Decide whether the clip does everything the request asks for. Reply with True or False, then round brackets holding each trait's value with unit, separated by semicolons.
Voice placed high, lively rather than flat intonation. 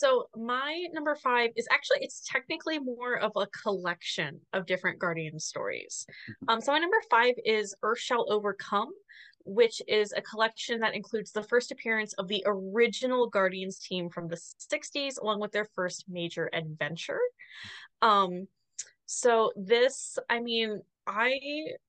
True (225 Hz; 6.8 semitones)